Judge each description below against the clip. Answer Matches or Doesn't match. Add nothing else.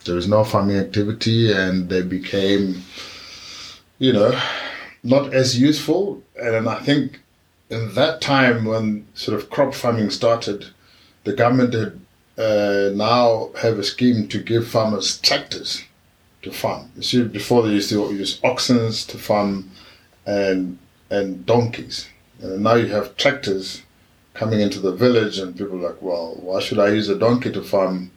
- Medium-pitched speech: Doesn't match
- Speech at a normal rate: Matches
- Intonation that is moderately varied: Matches